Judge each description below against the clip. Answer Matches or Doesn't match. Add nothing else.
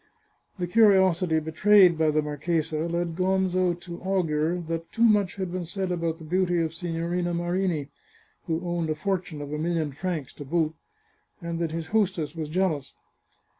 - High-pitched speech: Doesn't match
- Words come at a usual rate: Matches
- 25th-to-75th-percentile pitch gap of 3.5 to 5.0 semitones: Doesn't match